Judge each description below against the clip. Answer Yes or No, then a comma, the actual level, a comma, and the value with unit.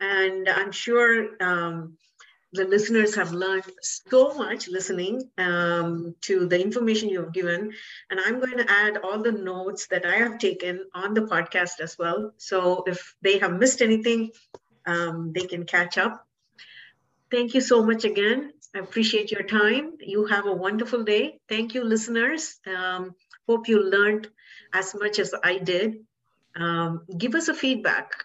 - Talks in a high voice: Yes, high, 200 Hz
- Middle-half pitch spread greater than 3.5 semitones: Yes, average, 3.9 semitones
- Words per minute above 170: No, average, 165 wpm